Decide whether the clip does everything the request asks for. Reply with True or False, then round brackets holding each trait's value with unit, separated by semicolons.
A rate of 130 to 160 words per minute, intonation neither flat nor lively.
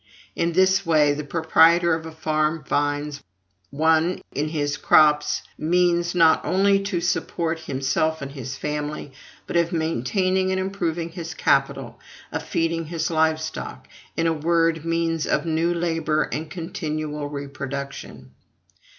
False (140 wpm; 2.2 semitones)